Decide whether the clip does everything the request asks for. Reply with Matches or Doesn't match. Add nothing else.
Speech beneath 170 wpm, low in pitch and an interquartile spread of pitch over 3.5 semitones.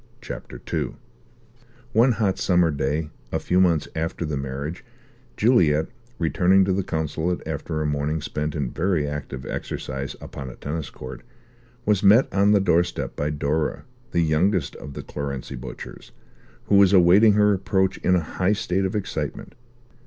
Matches